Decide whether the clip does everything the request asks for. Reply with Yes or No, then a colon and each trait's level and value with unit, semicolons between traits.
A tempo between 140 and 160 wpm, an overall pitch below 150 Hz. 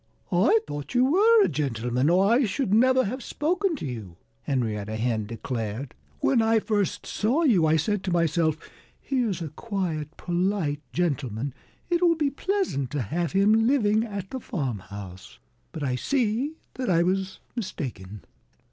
No: average, 155 wpm; medium, 180 Hz